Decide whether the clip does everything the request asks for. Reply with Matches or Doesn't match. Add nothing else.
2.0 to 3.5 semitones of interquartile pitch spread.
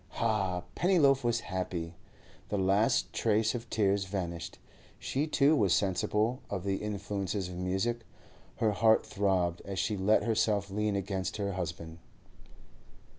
Matches